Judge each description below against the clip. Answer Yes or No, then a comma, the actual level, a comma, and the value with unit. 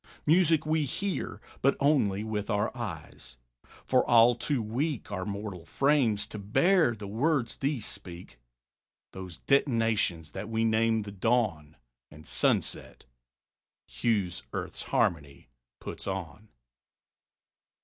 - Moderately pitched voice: No, low, 110 Hz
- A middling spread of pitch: No, wide, 5.8 semitones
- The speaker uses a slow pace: Yes, slow, 120 wpm